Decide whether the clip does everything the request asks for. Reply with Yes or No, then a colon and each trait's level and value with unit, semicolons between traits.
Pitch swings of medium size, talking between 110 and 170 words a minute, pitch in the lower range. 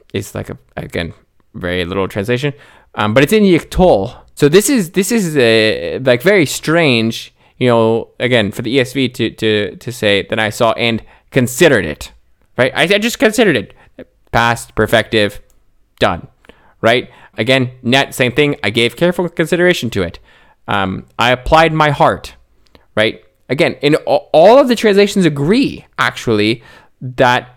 No: wide, 6.5 semitones; average, 155 wpm; low, 125 Hz